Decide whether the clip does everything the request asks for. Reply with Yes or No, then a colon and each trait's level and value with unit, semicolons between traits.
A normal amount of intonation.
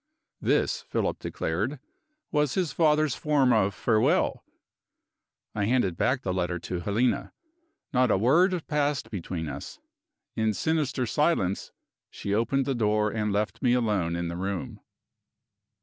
No: wide, 6.0 semitones